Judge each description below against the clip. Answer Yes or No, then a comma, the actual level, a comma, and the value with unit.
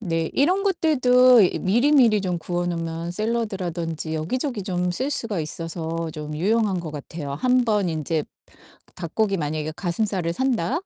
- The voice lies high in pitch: No, medium, 180 Hz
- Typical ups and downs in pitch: No, wide, 6.0 semitones